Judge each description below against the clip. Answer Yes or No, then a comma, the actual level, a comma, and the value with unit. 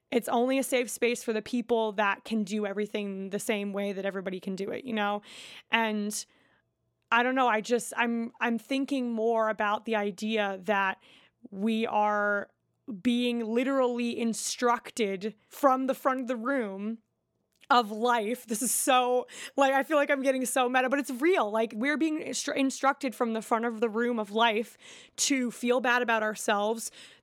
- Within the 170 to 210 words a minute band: Yes, average, 180 wpm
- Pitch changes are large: No, average, 3.0 semitones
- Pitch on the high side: Yes, high, 235 Hz